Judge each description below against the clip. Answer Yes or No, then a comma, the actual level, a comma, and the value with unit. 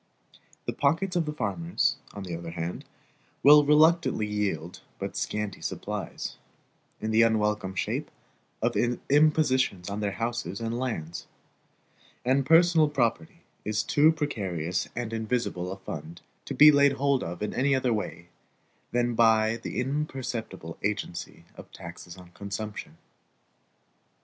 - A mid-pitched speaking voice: No, low, 115 Hz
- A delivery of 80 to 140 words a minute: Yes, slow, 135 wpm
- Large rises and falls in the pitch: Yes, wide, 6.6 semitones